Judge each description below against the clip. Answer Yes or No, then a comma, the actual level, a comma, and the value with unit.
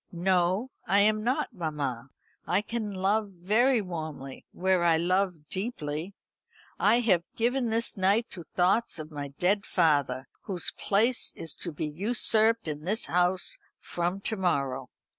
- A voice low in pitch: No, medium, 185 Hz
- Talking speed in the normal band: Yes, average, 145 wpm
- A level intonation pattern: No, average, 5.0 semitones